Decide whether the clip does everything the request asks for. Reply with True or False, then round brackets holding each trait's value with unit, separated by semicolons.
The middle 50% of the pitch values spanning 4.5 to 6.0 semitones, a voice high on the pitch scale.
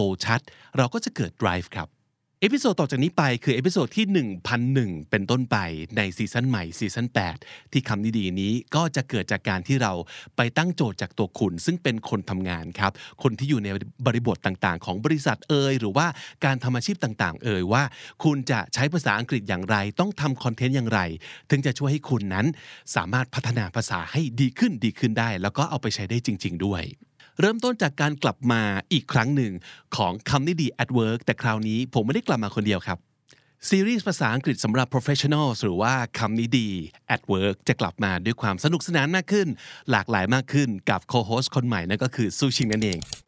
False (5.1 semitones; 120 Hz)